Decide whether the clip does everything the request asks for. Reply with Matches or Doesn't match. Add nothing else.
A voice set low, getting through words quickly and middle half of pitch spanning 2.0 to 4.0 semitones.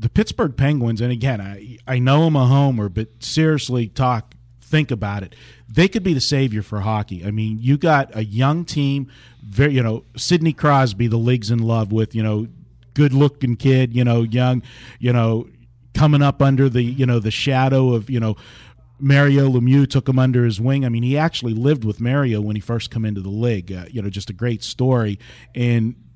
Matches